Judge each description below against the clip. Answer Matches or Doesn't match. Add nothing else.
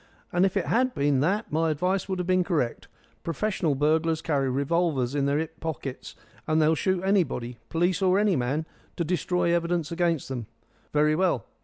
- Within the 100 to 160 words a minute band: Doesn't match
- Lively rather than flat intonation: Doesn't match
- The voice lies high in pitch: Doesn't match